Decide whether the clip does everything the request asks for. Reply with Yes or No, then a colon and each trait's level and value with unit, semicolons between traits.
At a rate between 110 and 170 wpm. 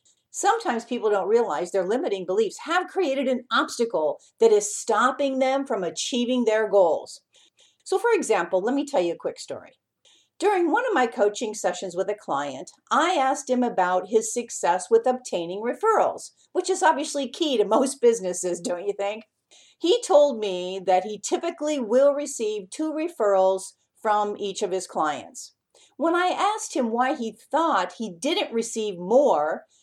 Yes: average, 165 wpm